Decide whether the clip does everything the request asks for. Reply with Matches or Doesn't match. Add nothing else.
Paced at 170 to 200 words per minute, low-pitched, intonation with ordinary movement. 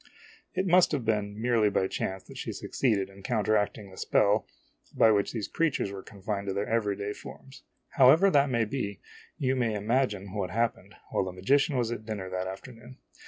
Matches